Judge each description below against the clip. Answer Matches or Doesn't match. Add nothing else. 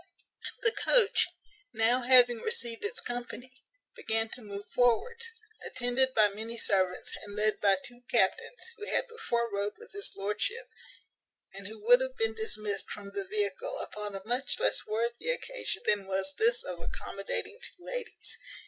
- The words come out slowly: Doesn't match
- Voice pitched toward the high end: Matches